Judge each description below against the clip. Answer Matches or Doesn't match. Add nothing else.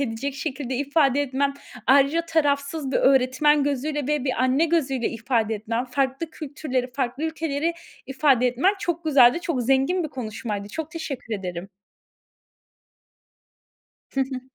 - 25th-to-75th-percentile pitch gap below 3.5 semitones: Matches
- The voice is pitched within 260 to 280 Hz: Matches